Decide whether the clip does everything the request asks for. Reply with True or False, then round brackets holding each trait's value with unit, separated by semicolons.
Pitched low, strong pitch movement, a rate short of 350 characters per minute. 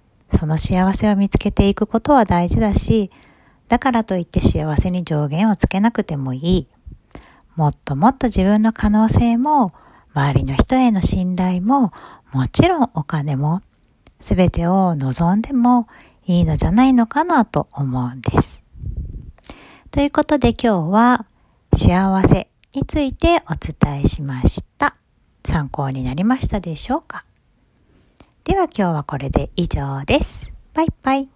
False (190 Hz; 7.7 semitones; 275 characters per minute)